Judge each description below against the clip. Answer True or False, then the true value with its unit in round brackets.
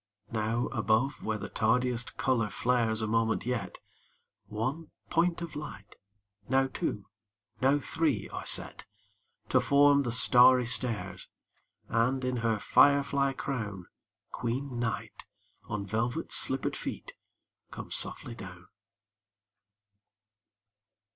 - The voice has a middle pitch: False (120 Hz)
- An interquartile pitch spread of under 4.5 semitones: True (3.5 semitones)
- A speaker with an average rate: False (115 wpm)